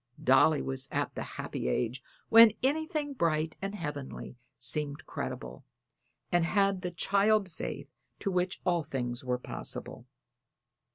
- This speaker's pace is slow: Yes, slow, 130 wpm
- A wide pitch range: Yes, wide, 6.9 semitones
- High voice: No, medium, 165 Hz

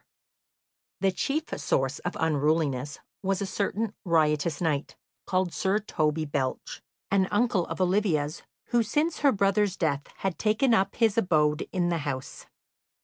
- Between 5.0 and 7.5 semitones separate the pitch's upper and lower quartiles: Yes, average, 5.3 semitones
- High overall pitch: No, medium, 180 Hz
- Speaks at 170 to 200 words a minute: No, average, 145 wpm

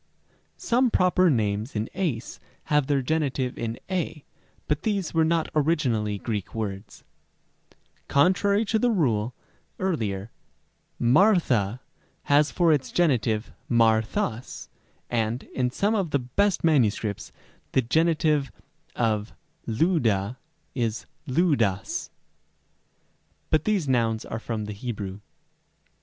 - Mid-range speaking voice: No, low, 130 Hz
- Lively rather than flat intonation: Yes, wide, 6.8 semitones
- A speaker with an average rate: No, slow, 120 wpm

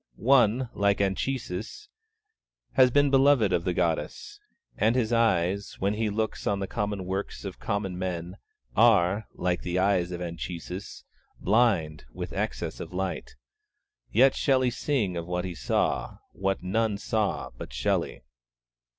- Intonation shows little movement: No, average, 4.0 semitones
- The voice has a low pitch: Yes, low, 100 Hz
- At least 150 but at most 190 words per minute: No, average, 140 wpm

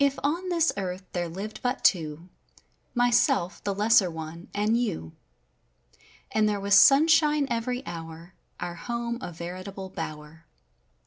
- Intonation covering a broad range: Yes, wide, 5.9 semitones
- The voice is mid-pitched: No, high, 200 Hz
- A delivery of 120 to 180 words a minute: Yes, average, 140 wpm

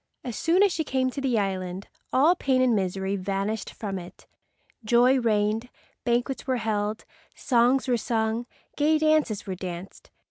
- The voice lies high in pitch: Yes, high, 235 Hz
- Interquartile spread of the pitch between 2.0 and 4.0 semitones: No, average, 4.6 semitones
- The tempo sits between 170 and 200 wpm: No, average, 155 wpm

